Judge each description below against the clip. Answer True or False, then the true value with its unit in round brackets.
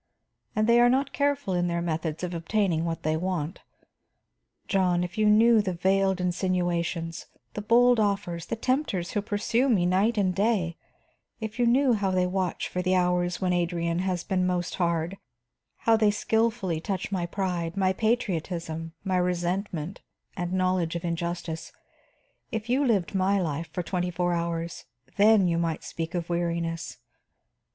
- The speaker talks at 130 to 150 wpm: False (160 wpm)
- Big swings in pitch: False (3.3 semitones)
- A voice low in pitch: False (180 Hz)